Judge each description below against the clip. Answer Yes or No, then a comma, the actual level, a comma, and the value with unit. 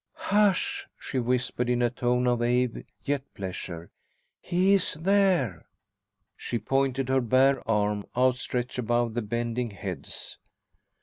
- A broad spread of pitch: No, narrow, 2.5 semitones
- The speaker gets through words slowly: Yes, slow, 125 wpm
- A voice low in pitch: Yes, low, 125 Hz